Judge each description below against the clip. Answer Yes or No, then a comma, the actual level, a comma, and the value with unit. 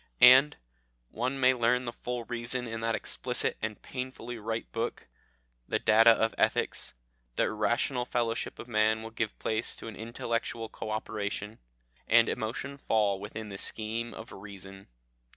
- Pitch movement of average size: No, narrow, 1.7 semitones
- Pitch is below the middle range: Yes, low, 115 Hz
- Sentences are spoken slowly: No, average, 150 wpm